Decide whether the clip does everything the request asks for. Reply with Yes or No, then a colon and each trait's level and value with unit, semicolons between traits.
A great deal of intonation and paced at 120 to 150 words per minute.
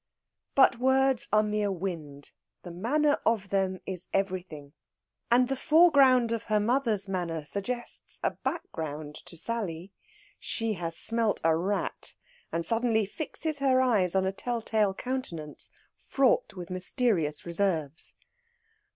Yes: wide, 6.0 semitones; slow, 135 wpm